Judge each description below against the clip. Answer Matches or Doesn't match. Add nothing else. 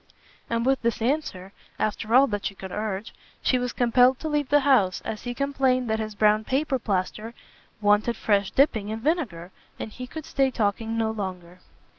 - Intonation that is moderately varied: Matches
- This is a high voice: Matches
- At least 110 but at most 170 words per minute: Doesn't match